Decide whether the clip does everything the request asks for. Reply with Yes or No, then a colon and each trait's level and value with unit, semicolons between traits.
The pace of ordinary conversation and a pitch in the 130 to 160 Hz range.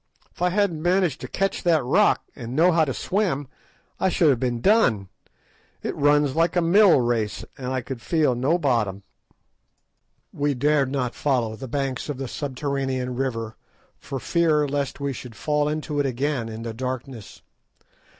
Yes: average, 170 wpm; medium, 140 Hz